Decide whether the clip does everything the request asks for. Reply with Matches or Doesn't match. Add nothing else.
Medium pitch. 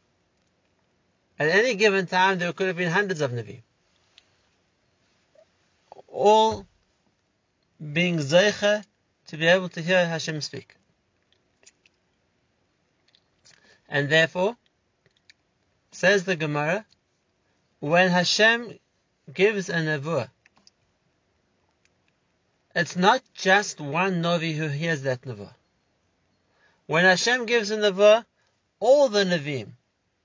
Matches